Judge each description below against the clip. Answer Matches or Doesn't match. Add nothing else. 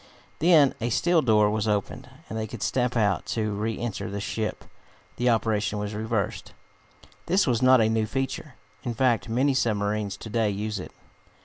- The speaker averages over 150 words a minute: Matches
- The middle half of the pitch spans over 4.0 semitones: Doesn't match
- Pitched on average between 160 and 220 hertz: Doesn't match